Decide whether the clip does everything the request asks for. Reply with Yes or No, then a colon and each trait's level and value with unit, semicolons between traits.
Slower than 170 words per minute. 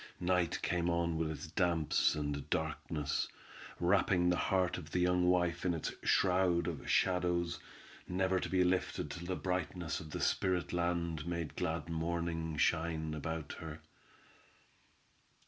Yes: average, 145 wpm